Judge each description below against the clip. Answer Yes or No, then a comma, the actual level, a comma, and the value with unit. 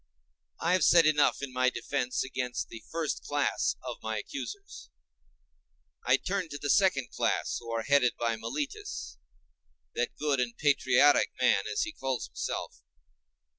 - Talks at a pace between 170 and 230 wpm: No, average, 150 wpm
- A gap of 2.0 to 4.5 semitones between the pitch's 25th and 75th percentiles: No, wide, 5.5 semitones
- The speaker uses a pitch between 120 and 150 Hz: Yes, medium, 140 Hz